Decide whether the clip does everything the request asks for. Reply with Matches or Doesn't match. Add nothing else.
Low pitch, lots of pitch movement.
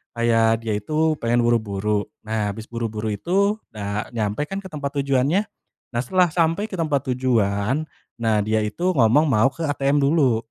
Matches